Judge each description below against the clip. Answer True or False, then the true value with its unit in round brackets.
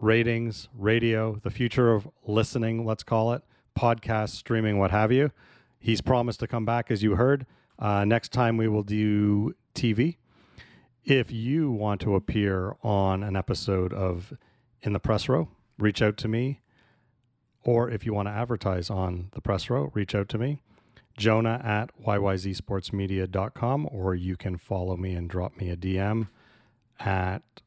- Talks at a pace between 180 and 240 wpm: False (160 wpm)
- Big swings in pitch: False (3.2 semitones)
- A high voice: False (110 Hz)